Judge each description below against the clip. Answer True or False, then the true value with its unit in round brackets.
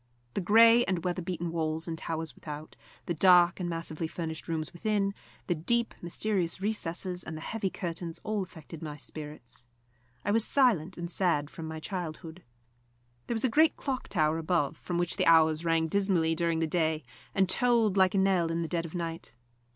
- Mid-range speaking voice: True (170 Hz)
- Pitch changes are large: False (3.0 semitones)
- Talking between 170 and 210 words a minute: True (190 wpm)